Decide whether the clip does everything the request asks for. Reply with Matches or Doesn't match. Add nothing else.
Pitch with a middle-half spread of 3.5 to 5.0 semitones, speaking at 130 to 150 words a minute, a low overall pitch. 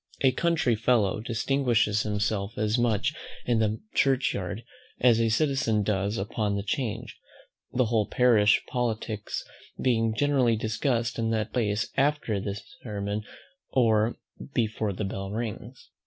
Doesn't match